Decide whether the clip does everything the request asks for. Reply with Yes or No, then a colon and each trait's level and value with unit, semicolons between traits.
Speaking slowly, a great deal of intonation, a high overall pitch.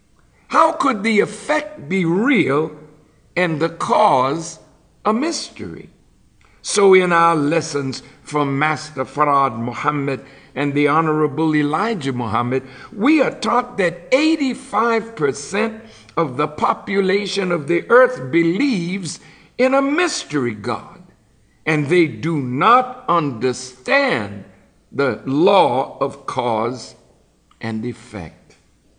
No: slow, 105 wpm; wide, 8.3 semitones; medium, 160 Hz